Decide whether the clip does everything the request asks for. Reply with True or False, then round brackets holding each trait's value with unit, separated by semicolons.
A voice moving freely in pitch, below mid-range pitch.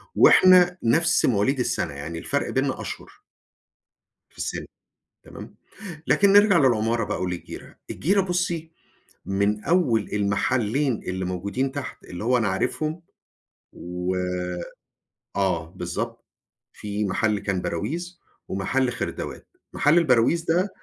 True (8.7 semitones; 120 Hz)